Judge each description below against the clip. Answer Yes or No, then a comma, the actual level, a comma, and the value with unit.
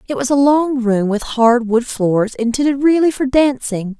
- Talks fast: No, average, 195 wpm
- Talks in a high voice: Yes, very high, 250 Hz